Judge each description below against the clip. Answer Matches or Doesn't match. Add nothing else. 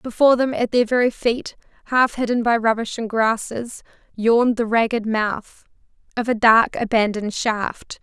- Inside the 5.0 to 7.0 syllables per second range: Doesn't match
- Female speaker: Matches